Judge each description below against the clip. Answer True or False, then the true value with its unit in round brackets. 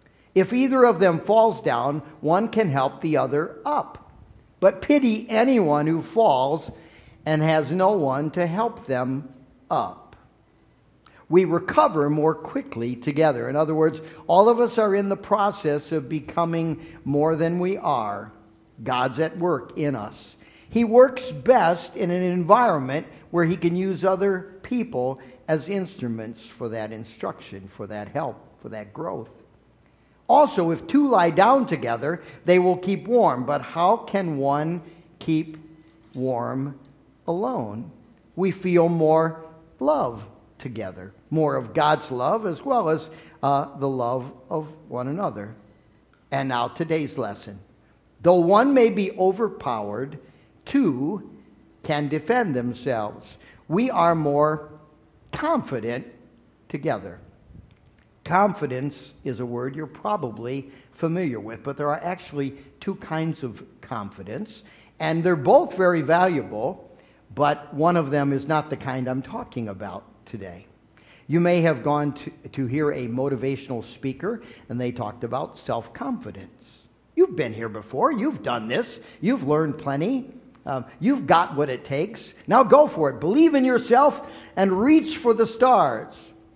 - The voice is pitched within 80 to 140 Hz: False (155 Hz)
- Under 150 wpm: True (140 wpm)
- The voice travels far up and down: True (6.3 semitones)